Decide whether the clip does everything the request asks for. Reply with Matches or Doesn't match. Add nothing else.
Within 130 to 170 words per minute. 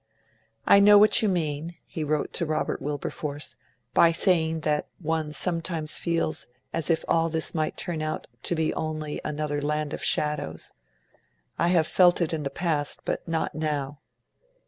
Matches